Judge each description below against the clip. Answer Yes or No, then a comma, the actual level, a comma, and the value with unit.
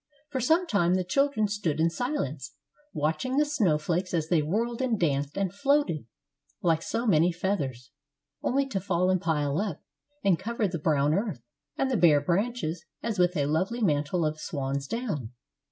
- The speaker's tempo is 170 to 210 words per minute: Yes, average, 175 wpm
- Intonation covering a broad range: Yes, wide, 6.5 semitones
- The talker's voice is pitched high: No, medium, 180 Hz